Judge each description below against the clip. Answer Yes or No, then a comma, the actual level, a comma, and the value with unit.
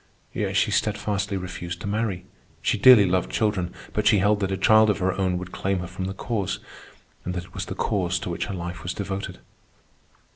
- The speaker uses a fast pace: Yes, fast, 215 wpm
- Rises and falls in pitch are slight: Yes, narrow, 2.2 semitones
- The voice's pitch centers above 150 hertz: No, very low, 95 Hz